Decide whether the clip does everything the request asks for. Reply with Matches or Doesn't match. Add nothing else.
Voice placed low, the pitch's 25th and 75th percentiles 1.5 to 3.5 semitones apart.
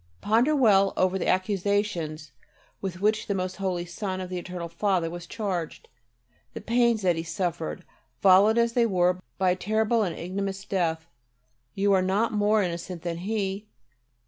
Doesn't match